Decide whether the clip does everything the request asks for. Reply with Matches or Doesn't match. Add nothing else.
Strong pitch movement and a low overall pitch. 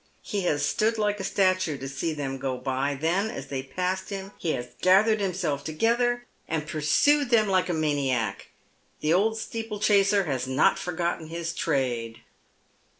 Doesn't match